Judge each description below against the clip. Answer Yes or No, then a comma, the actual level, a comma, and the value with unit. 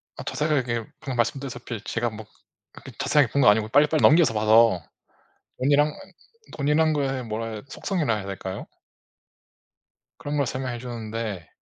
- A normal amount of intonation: Yes, average, 4.6 semitones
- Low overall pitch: Yes, low, 120 Hz